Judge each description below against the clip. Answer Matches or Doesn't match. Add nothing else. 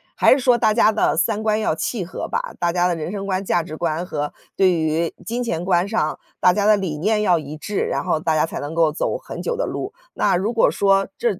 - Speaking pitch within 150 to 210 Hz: Matches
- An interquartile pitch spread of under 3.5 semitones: Doesn't match